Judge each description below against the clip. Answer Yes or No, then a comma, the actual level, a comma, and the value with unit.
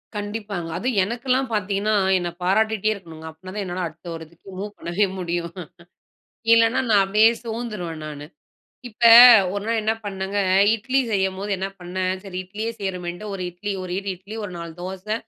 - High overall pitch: Yes, high, 195 Hz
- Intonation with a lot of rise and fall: No, average, 3.3 semitones